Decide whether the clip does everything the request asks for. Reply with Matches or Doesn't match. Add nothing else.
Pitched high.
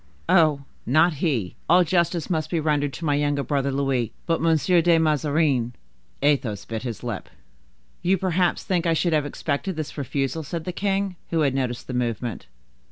Doesn't match